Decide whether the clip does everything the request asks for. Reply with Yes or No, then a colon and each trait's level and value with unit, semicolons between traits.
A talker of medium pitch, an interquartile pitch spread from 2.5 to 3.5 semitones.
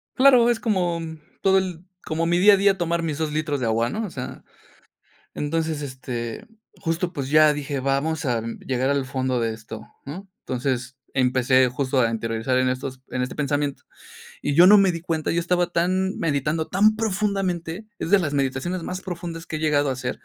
No: medium, 155 Hz; average, 5.3 semitones